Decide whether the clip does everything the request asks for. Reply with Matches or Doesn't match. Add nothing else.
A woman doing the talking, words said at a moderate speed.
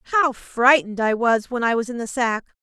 Doesn't match